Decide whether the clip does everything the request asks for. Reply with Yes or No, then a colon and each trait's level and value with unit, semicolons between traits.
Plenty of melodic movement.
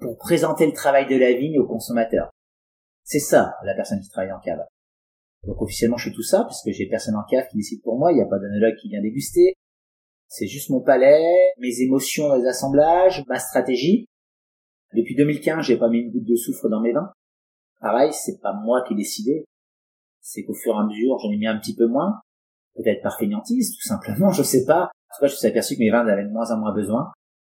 Yes: wide, 5.8 semitones